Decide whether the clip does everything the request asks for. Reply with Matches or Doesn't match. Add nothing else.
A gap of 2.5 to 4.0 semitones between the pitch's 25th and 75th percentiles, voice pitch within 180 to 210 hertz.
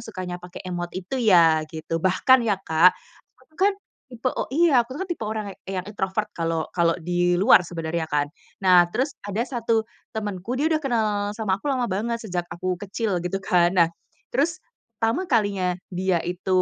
Doesn't match